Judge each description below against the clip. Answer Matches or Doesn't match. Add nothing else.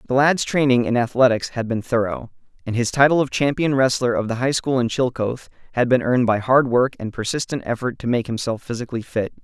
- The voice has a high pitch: Doesn't match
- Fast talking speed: Matches